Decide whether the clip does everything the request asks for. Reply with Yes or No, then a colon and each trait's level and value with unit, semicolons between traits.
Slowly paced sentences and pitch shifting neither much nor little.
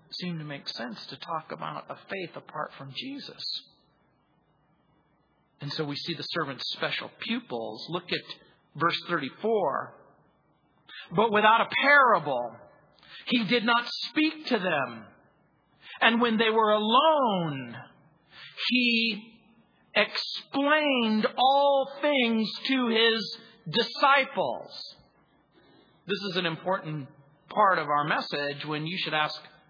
No: slow, 115 wpm; wide, 7.5 semitones